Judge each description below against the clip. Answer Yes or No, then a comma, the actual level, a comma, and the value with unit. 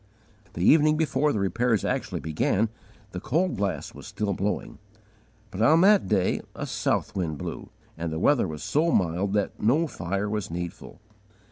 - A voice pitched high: No, low, 105 Hz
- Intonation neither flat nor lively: No, wide, 8.4 semitones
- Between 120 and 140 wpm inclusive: No, average, 165 wpm